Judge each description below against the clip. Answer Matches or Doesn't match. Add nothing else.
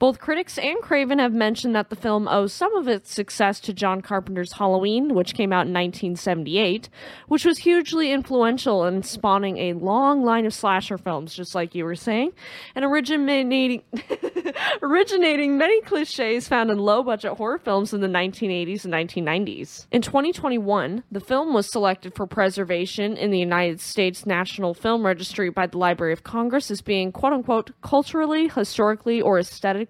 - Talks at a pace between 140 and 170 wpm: Matches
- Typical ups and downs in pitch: Doesn't match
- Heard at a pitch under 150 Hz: Doesn't match